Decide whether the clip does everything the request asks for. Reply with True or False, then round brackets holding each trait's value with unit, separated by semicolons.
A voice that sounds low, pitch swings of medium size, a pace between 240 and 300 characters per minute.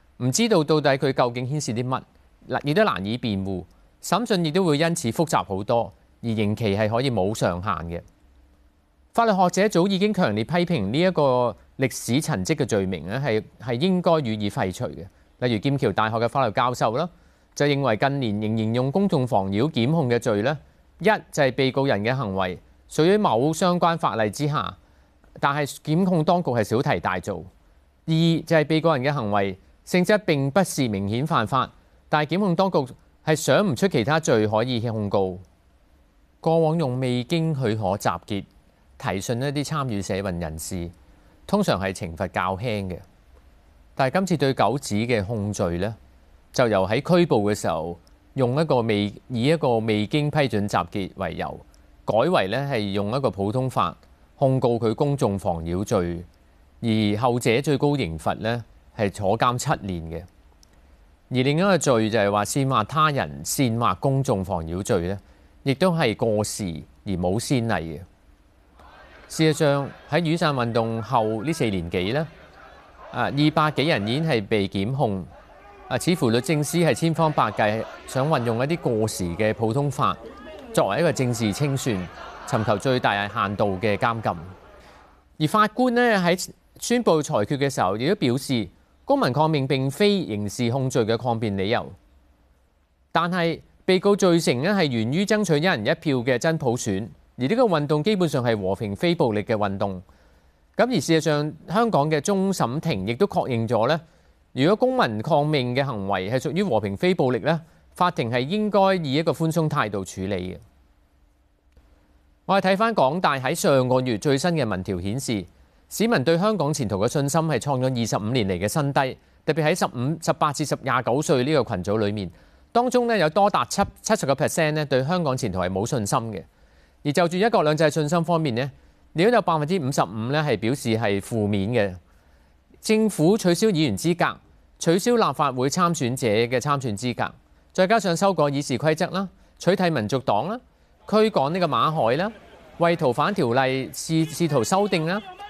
False (130 Hz; 8.1 semitones; 260 characters per minute)